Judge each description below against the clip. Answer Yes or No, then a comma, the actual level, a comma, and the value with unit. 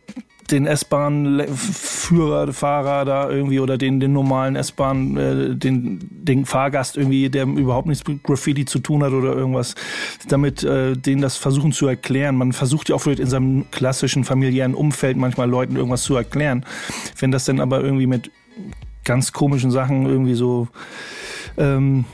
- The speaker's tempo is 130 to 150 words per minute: No, average, 160 wpm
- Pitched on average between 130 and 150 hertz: Yes, low, 135 Hz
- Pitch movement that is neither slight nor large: No, narrow, 1.6 semitones